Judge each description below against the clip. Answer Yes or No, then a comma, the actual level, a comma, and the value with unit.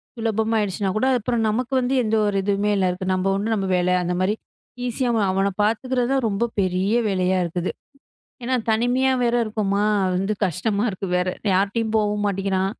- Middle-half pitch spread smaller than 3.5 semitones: Yes, average, 3.0 semitones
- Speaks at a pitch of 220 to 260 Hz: No, high, 205 Hz